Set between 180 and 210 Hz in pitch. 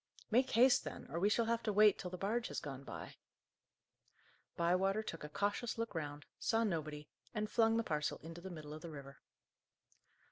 Yes: high, 190 Hz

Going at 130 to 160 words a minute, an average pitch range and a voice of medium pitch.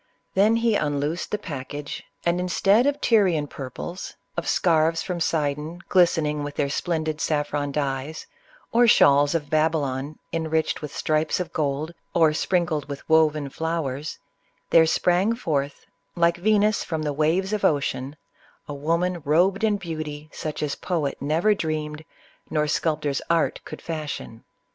Yes: average, 145 wpm; average, 3.0 semitones; medium, 155 Hz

